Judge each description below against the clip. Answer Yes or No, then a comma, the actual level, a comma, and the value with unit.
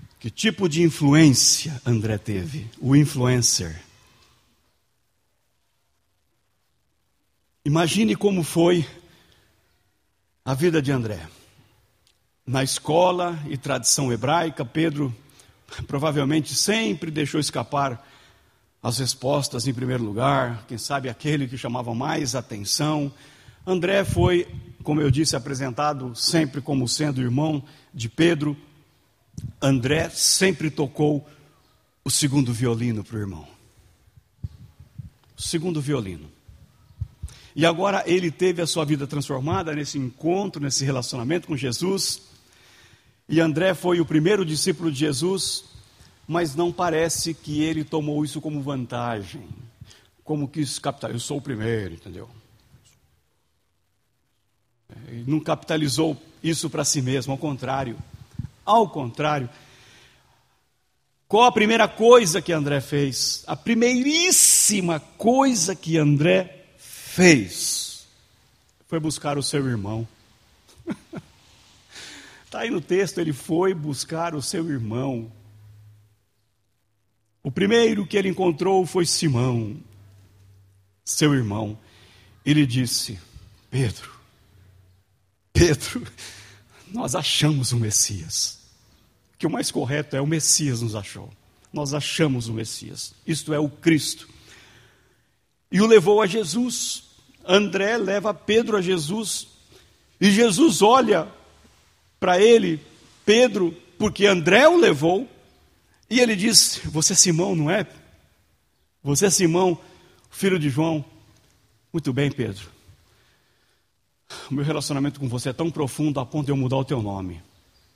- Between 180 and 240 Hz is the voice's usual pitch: No, medium, 140 Hz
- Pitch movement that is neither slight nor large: No, wide, 6.3 semitones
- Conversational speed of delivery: No, slow, 115 wpm